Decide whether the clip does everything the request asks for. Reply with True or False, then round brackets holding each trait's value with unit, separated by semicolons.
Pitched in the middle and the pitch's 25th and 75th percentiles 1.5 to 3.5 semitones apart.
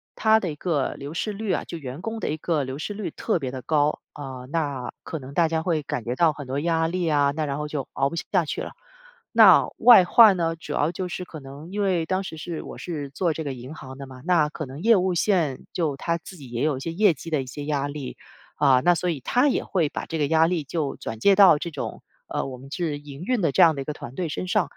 False (155 Hz; 4.0 semitones)